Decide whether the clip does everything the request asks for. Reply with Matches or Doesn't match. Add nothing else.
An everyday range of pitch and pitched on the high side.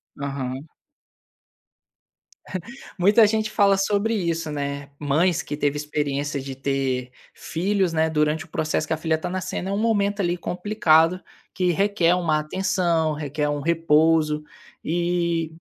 Doesn't match